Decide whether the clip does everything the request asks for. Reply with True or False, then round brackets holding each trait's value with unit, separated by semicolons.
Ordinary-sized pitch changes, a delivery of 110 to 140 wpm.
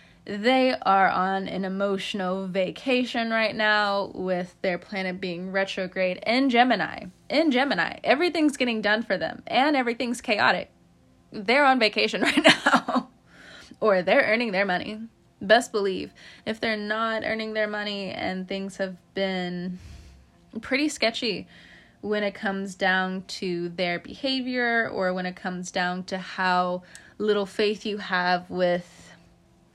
True (4.1 semitones; 135 wpm)